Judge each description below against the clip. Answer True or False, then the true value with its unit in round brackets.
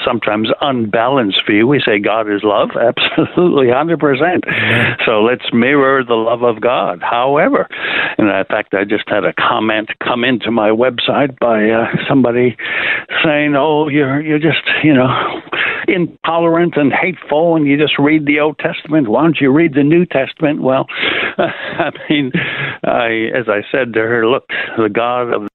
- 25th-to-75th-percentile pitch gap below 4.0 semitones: False (4.7 semitones)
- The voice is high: False (135 Hz)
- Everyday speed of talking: True (165 wpm)